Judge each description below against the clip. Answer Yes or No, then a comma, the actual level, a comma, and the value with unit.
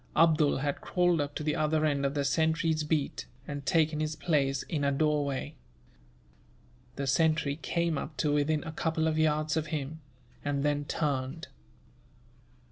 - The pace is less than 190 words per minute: Yes, average, 160 wpm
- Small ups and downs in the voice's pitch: Yes, narrow, 1.9 semitones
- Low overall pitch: No, medium, 150 Hz